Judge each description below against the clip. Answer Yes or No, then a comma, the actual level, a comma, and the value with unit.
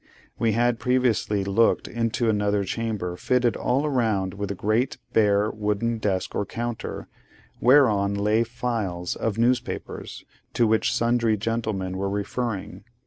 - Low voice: Yes, low, 110 Hz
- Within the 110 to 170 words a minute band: Yes, slow, 135 wpm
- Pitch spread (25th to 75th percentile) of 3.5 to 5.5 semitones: No, average, 2.7 semitones